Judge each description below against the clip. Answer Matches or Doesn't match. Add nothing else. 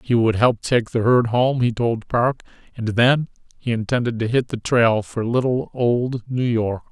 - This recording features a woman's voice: Doesn't match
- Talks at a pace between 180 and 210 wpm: Matches